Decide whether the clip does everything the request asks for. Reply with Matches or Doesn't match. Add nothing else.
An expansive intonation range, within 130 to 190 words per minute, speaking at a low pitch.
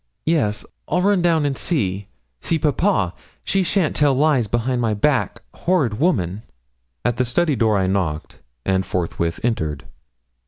Matches